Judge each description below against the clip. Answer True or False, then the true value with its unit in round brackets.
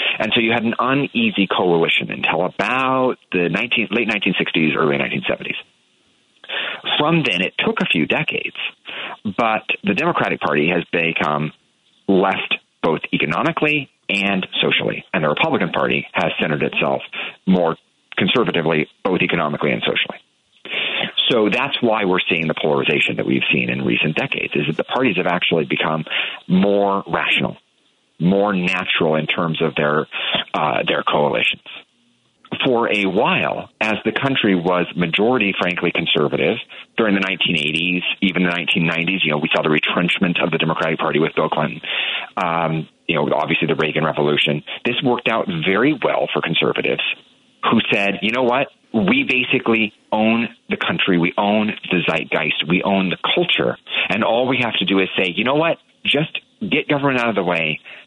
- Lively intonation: True (5.8 semitones)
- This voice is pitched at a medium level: False (95 Hz)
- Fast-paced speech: False (165 wpm)